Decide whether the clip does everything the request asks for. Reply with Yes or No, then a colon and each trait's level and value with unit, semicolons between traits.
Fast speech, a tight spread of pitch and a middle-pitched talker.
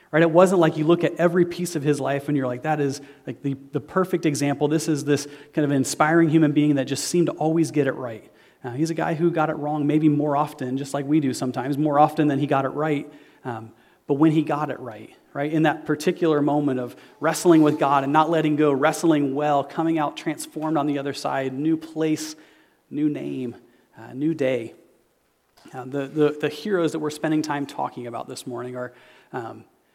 Yes: fast, 225 wpm; narrow, 2.1 semitones; medium, 150 Hz